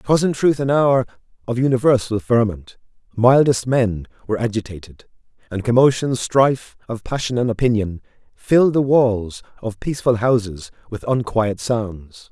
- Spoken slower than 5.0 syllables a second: Yes, 4.8 syllables/s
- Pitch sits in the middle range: No, low, 115 Hz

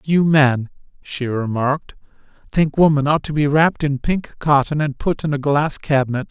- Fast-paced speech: No, average, 180 wpm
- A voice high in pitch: No, medium, 145 Hz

